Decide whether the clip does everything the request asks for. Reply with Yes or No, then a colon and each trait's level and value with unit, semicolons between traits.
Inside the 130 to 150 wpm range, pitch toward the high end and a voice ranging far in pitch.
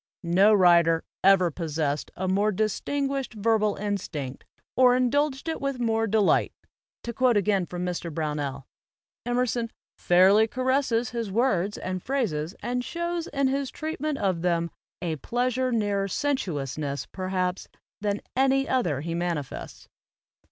Yes: slow, 135 wpm; high, 205 Hz; wide, 6.5 semitones